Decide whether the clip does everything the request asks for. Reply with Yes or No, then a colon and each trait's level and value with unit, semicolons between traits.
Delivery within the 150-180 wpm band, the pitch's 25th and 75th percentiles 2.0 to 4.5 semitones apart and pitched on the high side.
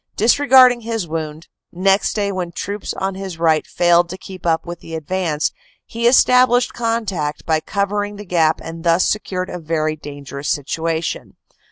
No: average, 170 wpm; average, 4.2 semitones; medium, 180 Hz